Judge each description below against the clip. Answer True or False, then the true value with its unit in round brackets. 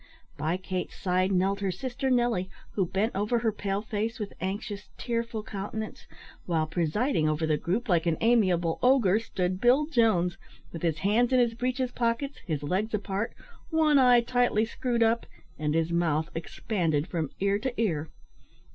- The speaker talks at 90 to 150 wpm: False (165 wpm)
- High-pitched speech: True (200 Hz)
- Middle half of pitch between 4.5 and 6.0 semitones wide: True (5.3 semitones)